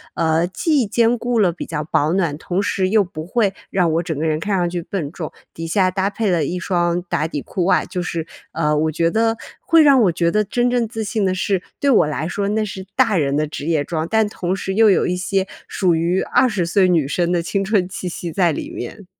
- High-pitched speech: No, medium, 180 Hz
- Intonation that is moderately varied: Yes, average, 3.9 semitones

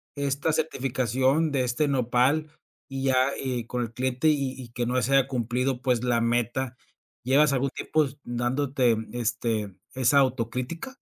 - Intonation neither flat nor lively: No, narrow, 2.2 semitones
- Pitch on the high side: No, low, 130 Hz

